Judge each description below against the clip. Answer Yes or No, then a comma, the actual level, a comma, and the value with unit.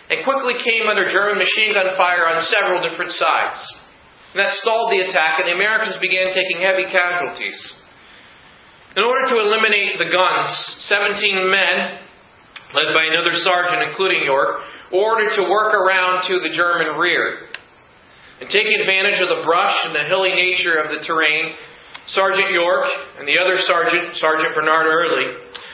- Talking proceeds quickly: No, average, 160 wpm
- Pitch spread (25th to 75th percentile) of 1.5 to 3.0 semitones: Yes, average, 2.7 semitones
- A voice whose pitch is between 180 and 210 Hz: Yes, medium, 185 Hz